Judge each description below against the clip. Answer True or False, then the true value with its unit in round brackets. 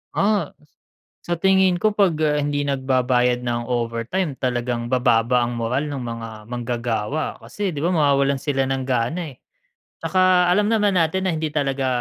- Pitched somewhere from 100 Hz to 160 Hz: True (140 Hz)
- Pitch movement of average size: False (6.0 semitones)